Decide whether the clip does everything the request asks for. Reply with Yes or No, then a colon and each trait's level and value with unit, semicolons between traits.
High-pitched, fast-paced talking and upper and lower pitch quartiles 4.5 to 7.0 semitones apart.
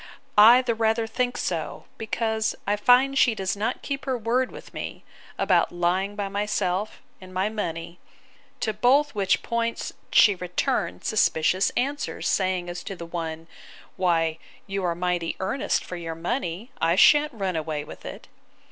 No: high, 200 Hz; average, 160 wpm; average, 4.8 semitones